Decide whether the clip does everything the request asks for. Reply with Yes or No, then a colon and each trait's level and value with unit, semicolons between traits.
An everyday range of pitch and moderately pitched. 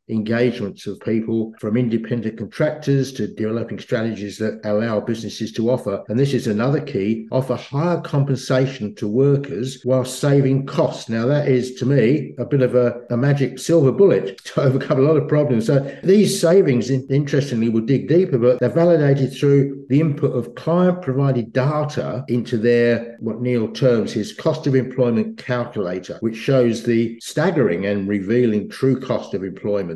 No: average, 3.5 semitones; low, 125 Hz